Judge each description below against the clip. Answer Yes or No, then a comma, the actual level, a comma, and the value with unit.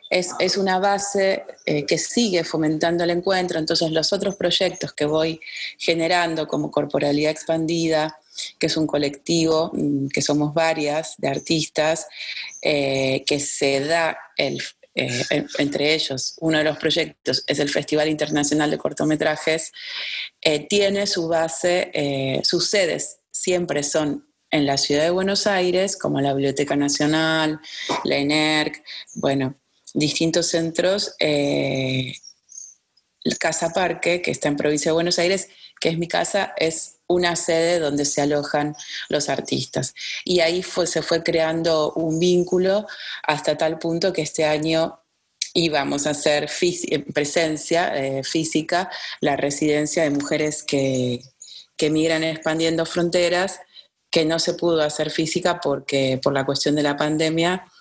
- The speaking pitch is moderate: Yes, medium, 160 Hz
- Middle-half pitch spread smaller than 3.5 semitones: Yes, narrow, 2.6 semitones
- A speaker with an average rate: Yes, average, 140 wpm